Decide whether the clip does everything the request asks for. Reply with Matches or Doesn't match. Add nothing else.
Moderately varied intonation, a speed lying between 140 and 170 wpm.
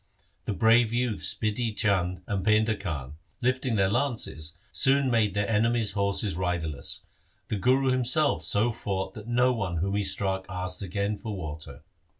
Matches